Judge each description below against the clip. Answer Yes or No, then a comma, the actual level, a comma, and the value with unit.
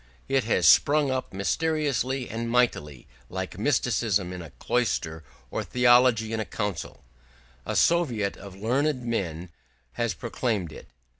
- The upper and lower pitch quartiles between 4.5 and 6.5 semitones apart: Yes, average, 5.0 semitones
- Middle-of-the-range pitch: No, low, 115 Hz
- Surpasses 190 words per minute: No, slow, 135 wpm